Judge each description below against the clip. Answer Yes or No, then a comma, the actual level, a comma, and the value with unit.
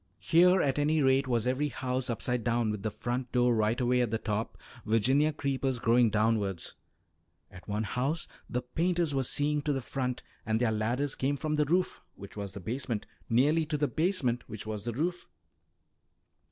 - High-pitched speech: No, low, 125 Hz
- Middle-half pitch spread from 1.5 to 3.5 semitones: No, average, 4.5 semitones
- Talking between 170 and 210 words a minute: Yes, average, 185 wpm